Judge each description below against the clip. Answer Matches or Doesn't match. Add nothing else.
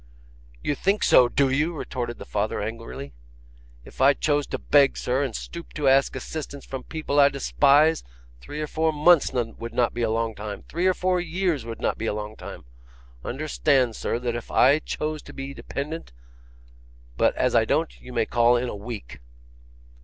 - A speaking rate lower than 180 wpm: Doesn't match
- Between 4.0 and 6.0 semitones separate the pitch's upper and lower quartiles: Matches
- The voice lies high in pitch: Doesn't match